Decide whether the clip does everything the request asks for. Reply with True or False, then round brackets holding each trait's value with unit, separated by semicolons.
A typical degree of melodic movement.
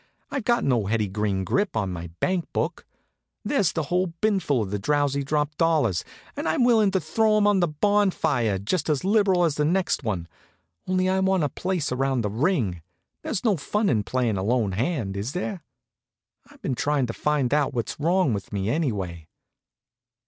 False (9.0 semitones)